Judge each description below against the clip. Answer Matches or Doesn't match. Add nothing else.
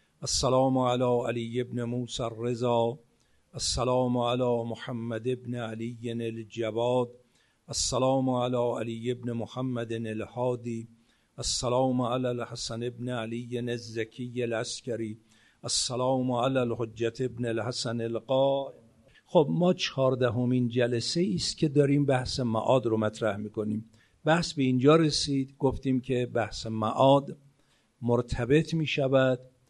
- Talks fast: Doesn't match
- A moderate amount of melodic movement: Doesn't match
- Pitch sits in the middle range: Doesn't match